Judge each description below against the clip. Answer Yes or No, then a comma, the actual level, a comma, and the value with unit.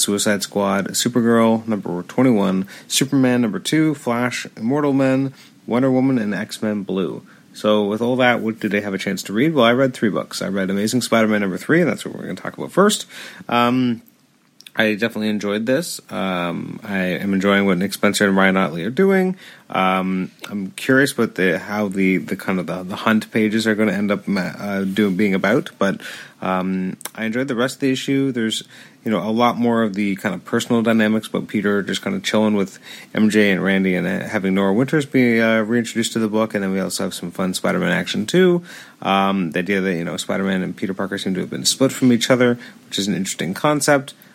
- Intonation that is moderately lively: Yes, average, 4.2 semitones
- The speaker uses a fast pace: Yes, fast, 225 wpm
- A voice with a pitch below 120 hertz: Yes, low, 110 Hz